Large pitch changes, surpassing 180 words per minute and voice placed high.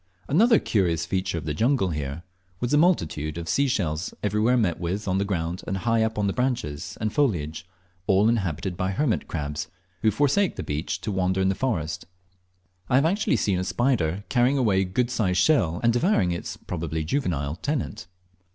No: wide, 6.5 semitones; average, 190 wpm; very low, 95 Hz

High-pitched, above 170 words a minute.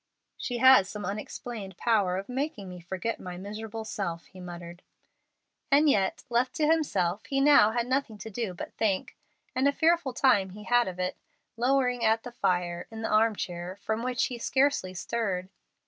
Yes: high, 220 Hz; average, 180 wpm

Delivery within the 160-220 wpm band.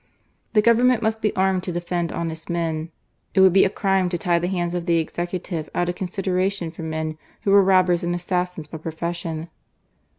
Yes: average, 195 wpm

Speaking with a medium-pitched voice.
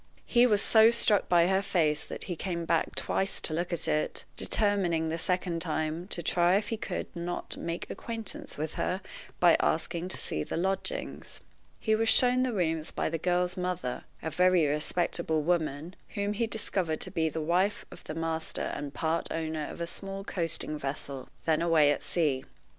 Yes: medium, 170 Hz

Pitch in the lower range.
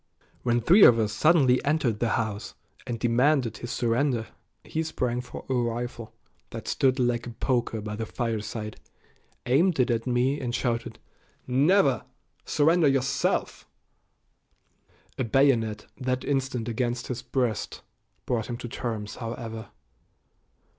Yes: low, 120 Hz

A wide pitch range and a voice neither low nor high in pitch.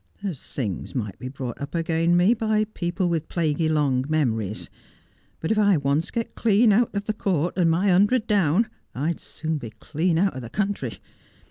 Yes: wide, 6.0 semitones; medium, 165 Hz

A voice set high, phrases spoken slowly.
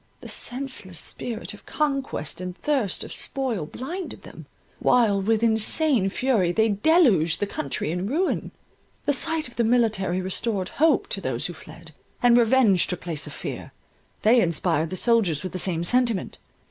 No: high, 220 Hz; average, 165 wpm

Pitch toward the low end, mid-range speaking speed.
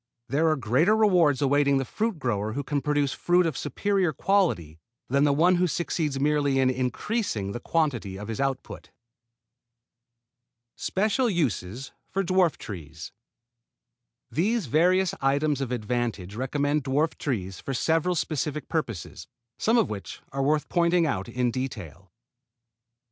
No: medium, 145 Hz; average, 145 wpm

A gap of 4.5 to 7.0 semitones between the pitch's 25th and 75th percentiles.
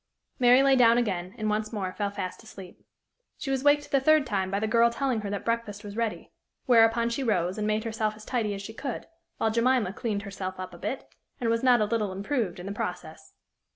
No: average, 3.1 semitones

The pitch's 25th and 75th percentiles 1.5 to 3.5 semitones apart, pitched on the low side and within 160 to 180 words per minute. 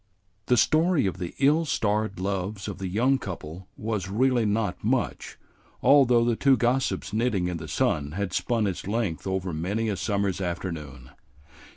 No: average, 4.5 semitones; low, 100 Hz; average, 165 wpm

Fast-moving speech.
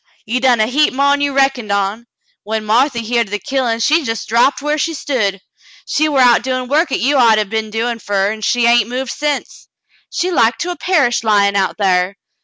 Yes: fast, 225 wpm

